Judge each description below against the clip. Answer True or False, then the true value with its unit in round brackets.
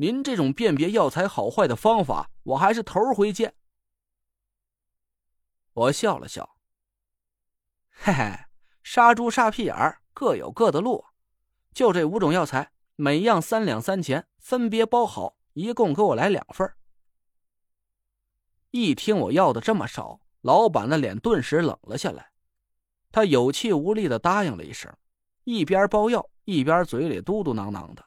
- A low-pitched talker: False (165 Hz)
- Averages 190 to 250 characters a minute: True (215 characters per minute)